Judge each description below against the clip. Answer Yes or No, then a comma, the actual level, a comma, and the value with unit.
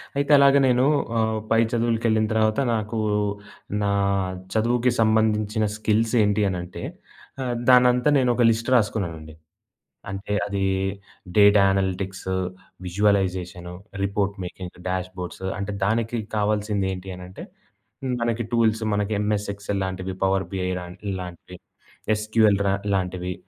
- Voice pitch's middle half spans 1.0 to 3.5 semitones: Yes, average, 2.9 semitones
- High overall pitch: No, low, 105 Hz